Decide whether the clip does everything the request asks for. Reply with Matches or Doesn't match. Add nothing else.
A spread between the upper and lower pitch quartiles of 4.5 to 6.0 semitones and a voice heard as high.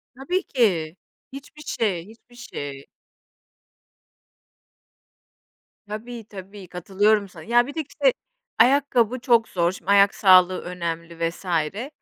Matches